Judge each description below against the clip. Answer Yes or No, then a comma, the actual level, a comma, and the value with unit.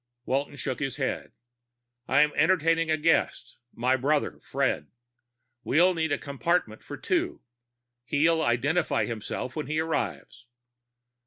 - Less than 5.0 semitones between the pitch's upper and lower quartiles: Yes, average, 3.8 semitones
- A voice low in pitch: No, medium, 150 Hz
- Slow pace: Yes, slow, 125 wpm